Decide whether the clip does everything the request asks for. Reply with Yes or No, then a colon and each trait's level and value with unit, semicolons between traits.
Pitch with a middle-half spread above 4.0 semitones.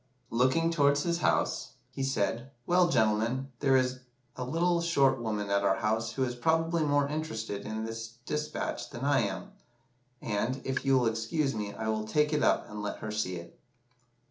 Yes: average, 5.2 semitones